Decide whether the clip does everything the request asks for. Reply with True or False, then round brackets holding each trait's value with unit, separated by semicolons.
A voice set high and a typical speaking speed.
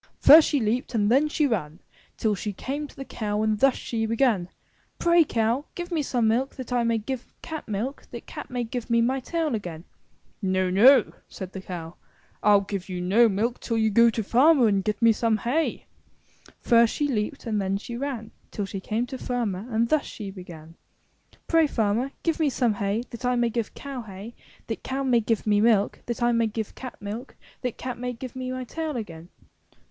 False (230 Hz; 220 wpm)